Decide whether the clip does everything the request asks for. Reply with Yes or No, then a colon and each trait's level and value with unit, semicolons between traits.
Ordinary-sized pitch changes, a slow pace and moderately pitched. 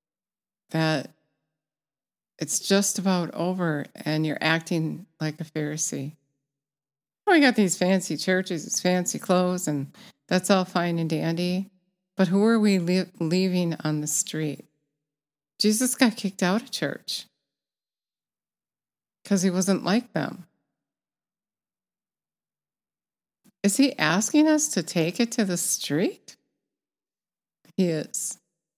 Yes: average, 4.1 semitones; slow, 120 wpm; medium, 180 Hz